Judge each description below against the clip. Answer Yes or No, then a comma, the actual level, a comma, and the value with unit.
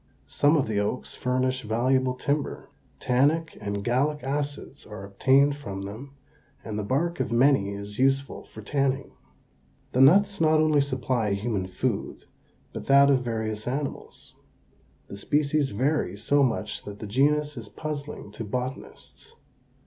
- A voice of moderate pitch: No, low, 130 Hz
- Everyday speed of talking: Yes, average, 145 wpm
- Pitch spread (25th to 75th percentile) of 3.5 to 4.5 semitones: No, average, 5.0 semitones